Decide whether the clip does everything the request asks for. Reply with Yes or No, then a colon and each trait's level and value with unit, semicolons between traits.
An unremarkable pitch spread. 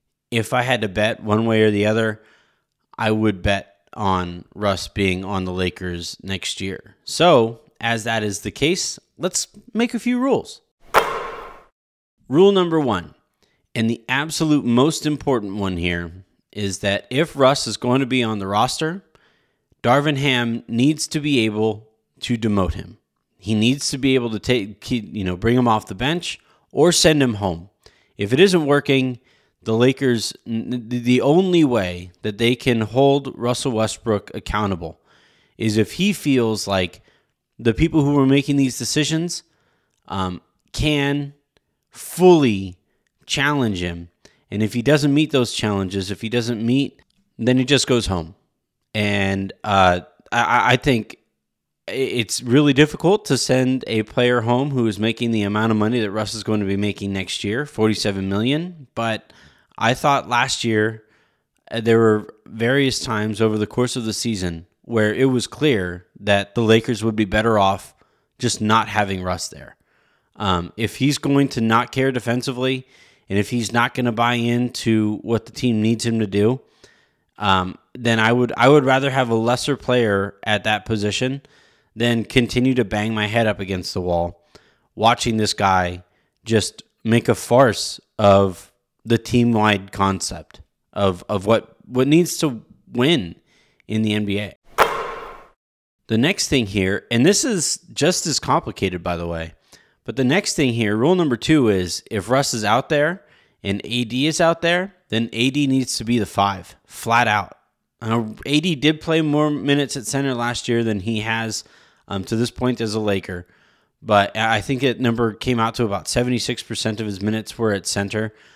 Yes: average, 4.2 semitones